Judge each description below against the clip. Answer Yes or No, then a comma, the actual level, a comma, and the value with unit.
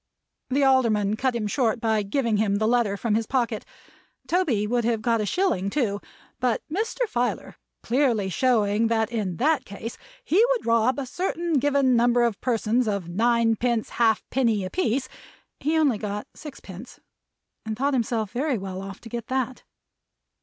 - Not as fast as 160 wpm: No, average, 165 wpm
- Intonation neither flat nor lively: Yes, average, 3.6 semitones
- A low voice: No, high, 235 Hz